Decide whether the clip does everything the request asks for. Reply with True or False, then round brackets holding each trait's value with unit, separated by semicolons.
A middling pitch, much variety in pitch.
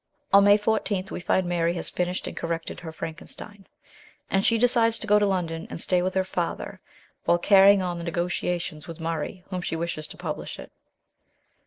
False (180 Hz; 2.9 semitones)